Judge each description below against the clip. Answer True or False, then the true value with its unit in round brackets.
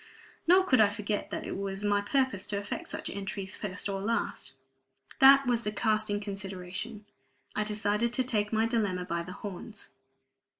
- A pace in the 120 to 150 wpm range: False (170 wpm)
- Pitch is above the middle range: True (205 Hz)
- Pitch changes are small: True (2.3 semitones)